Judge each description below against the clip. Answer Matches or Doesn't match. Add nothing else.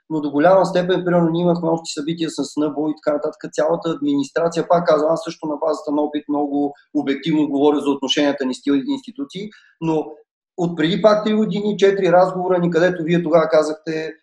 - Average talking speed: Doesn't match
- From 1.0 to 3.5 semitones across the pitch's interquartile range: Matches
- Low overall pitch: Doesn't match